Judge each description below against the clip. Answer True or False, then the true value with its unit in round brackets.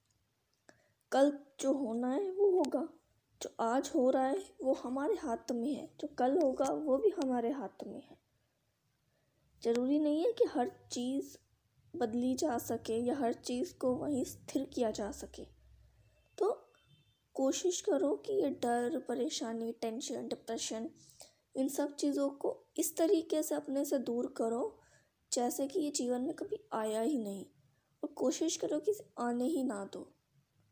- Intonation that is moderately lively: True (4.6 semitones)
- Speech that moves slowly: False (160 wpm)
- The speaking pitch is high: True (275 Hz)